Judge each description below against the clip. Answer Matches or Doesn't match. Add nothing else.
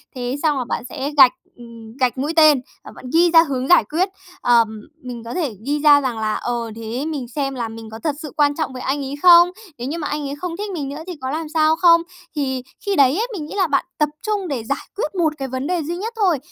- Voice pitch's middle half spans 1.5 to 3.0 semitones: Doesn't match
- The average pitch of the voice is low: Doesn't match